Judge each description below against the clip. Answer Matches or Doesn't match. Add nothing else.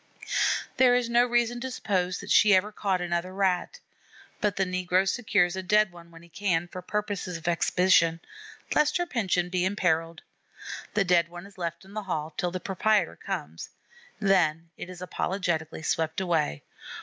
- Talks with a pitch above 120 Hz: Matches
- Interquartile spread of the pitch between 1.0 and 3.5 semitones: Matches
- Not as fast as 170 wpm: Doesn't match